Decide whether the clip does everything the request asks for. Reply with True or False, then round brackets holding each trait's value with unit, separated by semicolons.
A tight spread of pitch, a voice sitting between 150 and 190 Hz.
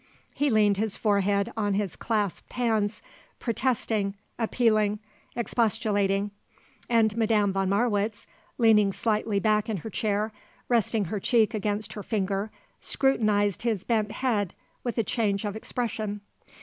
False (1.8 semitones; 215 Hz)